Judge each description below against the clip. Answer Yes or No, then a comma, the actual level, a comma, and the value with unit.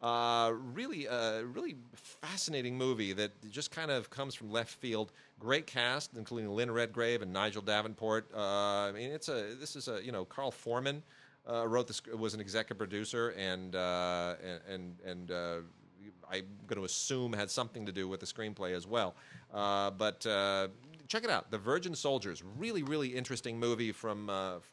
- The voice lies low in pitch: Yes, low, 110 Hz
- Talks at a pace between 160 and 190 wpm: Yes, average, 180 wpm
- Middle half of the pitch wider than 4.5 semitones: No, average, 3.7 semitones